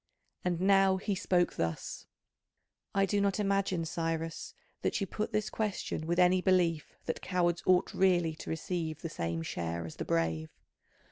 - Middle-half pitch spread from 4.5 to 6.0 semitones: No, average, 3.1 semitones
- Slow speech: No, average, 160 wpm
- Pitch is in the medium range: Yes, medium, 175 Hz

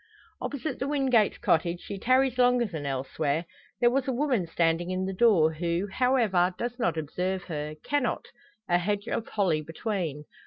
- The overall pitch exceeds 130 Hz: Yes, high, 190 Hz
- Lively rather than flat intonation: Yes, wide, 6.8 semitones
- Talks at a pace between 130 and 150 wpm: No, average, 165 wpm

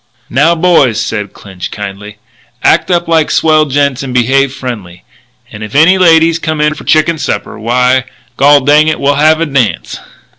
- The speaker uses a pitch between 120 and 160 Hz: Yes, medium, 140 Hz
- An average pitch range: Yes, average, 4.6 semitones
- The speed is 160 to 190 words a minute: Yes, average, 180 wpm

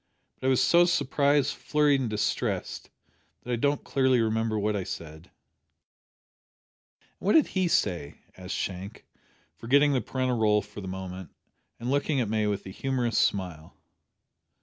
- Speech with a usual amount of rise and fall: No, wide, 5.8 semitones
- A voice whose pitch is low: Yes, low, 115 Hz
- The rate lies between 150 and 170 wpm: Yes, average, 155 wpm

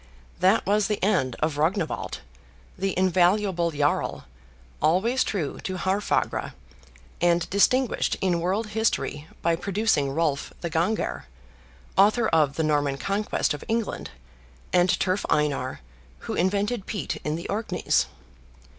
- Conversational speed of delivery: No, slow, 125 wpm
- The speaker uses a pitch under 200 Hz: Yes, medium, 185 Hz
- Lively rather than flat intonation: No, average, 4.7 semitones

